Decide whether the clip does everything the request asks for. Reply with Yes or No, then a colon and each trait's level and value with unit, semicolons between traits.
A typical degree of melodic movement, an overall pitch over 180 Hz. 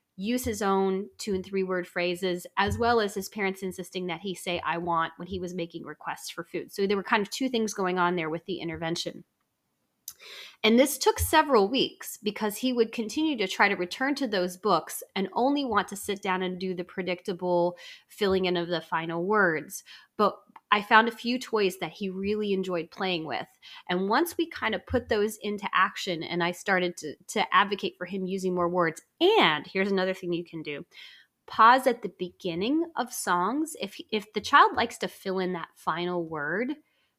Yes: average, 3.8 semitones; high, 190 Hz